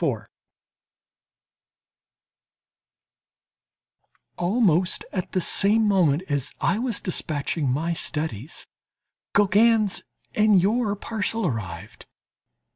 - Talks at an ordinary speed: No, slow, 75 wpm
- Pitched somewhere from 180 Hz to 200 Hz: Yes, medium, 185 Hz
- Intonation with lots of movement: Yes, wide, 5.7 semitones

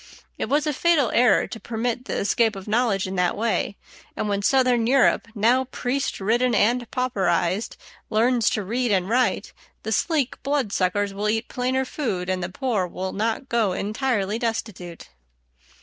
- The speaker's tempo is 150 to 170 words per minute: Yes, average, 165 wpm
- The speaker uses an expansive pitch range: No, average, 4.0 semitones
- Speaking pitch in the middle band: No, high, 225 Hz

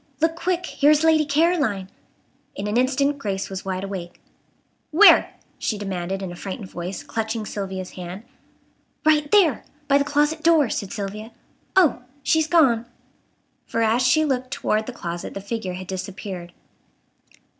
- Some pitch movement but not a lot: No, wide, 7.4 semitones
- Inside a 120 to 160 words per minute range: Yes, average, 155 wpm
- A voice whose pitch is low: No, high, 225 Hz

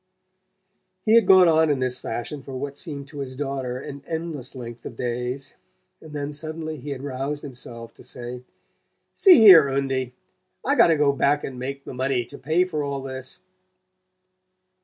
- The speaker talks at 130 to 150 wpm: No, average, 180 wpm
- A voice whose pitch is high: No, medium, 140 Hz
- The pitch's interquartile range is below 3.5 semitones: Yes, average, 2.8 semitones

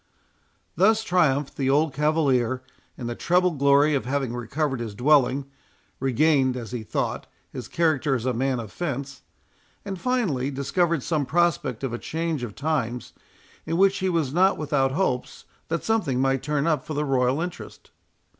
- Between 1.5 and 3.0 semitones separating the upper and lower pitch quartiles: No, average, 4.1 semitones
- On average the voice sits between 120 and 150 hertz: Yes, medium, 140 Hz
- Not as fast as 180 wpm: Yes, average, 165 wpm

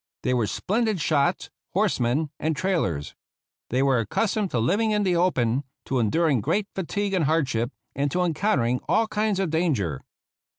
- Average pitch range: No, wide, 7.5 semitones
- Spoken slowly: No, average, 165 wpm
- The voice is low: No, medium, 160 Hz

